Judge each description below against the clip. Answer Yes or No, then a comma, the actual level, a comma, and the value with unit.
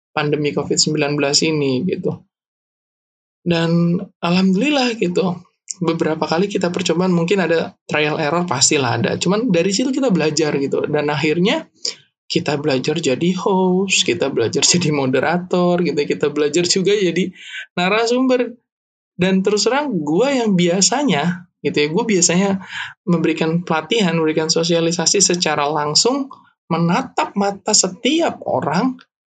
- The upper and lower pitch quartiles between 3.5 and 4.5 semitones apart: Yes, average, 4.0 semitones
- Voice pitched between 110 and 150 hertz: No, medium, 175 Hz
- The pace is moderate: Yes, average, 120 wpm